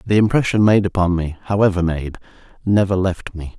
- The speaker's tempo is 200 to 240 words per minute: No, average, 170 wpm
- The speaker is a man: Yes, male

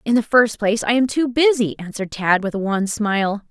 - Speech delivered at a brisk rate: Yes, fast, 240 wpm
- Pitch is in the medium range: No, high, 220 Hz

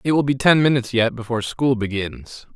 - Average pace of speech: No, fast, 210 wpm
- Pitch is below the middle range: Yes, low, 125 Hz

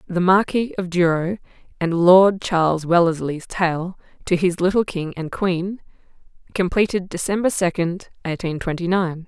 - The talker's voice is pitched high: No, medium, 180 Hz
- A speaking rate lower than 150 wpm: Yes, slow, 135 wpm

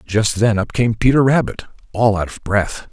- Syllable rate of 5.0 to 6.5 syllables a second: No, 4.7 syllables/s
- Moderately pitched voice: No, low, 110 Hz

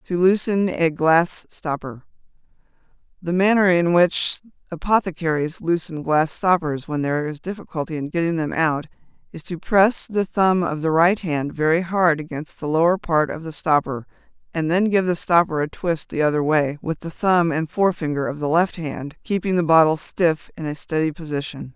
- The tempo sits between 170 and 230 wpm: Yes, average, 180 wpm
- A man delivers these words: No, female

